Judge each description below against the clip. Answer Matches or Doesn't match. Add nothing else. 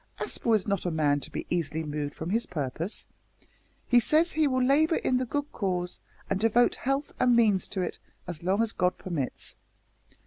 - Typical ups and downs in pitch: Doesn't match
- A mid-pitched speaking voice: Doesn't match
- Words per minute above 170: Matches